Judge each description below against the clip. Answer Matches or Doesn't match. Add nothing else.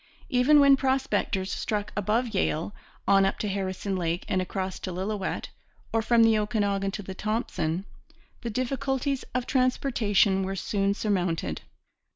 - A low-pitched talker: Doesn't match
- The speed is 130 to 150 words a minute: Matches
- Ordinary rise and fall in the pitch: Matches